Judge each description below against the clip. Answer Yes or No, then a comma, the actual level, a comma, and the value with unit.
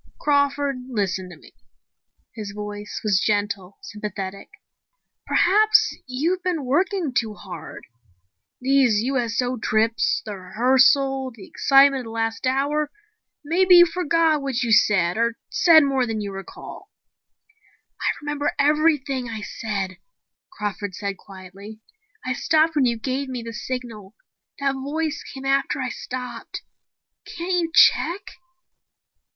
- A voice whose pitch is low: No, very high, 255 Hz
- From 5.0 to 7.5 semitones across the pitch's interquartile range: Yes, wide, 5.4 semitones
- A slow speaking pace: Yes, slow, 130 wpm